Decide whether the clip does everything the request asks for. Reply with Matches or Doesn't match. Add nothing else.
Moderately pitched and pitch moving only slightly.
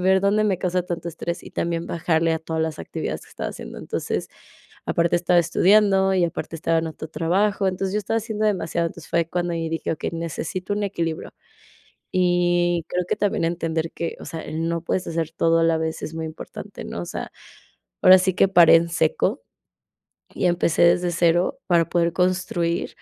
Matches